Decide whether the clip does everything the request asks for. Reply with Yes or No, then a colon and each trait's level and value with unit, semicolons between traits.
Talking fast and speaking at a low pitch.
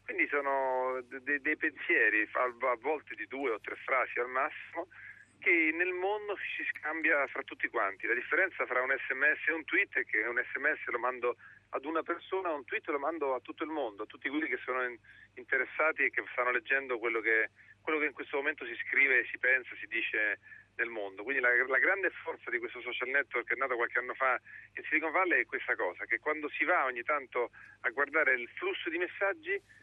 No: fast, 210 wpm; medium, 160 Hz